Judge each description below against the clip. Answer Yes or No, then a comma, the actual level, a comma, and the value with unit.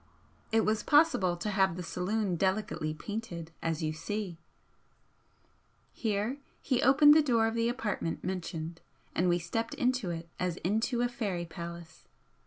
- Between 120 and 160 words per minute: Yes, average, 150 wpm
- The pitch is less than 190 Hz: No, high, 200 Hz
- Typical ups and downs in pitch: Yes, average, 4.9 semitones